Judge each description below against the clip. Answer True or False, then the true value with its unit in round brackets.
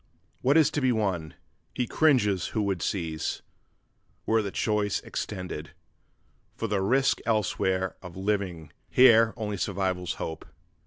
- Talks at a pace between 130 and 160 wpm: True (135 wpm)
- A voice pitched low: True (100 Hz)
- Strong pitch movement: False (3.6 semitones)